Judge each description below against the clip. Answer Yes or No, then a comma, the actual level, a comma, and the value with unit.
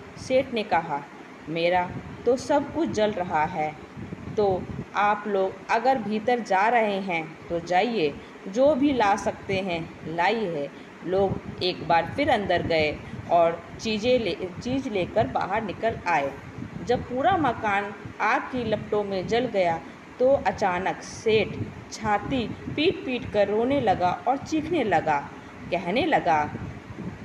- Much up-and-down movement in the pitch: Yes, wide, 6.3 semitones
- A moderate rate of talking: Yes, average, 140 wpm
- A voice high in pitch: Yes, high, 205 Hz